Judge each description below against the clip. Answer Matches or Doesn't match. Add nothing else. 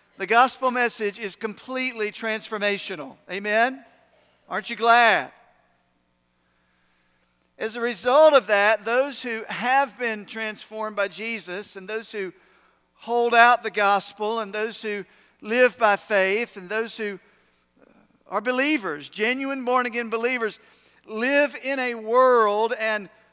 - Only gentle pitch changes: Doesn't match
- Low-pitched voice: Doesn't match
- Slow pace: Matches